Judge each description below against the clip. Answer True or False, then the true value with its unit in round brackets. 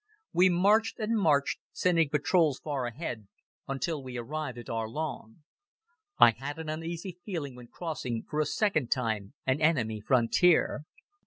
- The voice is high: False (145 Hz)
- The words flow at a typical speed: True (145 wpm)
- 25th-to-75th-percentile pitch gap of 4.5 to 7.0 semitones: True (5.4 semitones)